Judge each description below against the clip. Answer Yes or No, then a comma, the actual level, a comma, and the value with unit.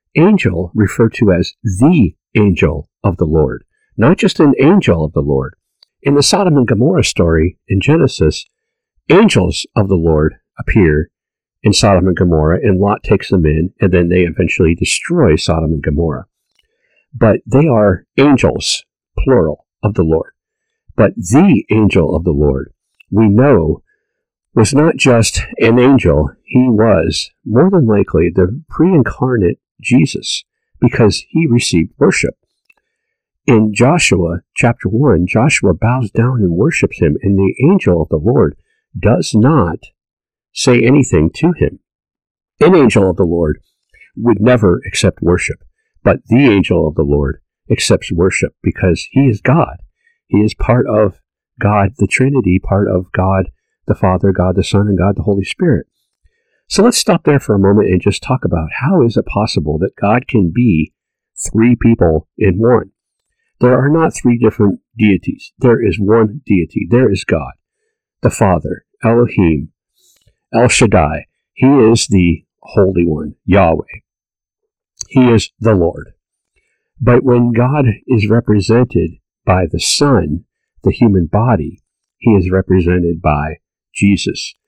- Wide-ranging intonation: Yes, wide, 6.1 semitones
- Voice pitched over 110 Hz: No, low, 105 Hz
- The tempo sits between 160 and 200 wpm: No, average, 150 wpm